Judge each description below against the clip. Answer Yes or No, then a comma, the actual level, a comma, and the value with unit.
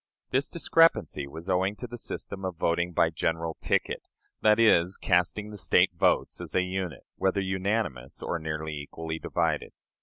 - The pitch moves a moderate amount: Yes, average, 3.7 semitones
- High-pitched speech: No, very low, 90 Hz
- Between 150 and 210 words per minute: Yes, average, 160 wpm